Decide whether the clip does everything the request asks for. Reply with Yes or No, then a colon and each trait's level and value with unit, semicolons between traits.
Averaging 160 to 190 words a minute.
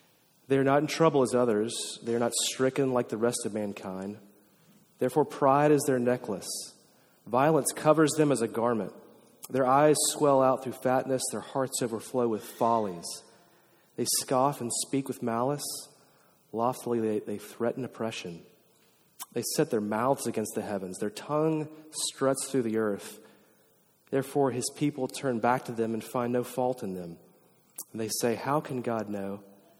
Yes: average, 165 wpm